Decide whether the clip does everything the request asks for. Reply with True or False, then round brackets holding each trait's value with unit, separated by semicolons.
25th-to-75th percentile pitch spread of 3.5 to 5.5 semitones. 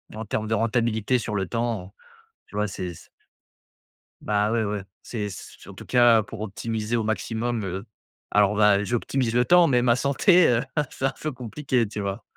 False (2.7 semitones)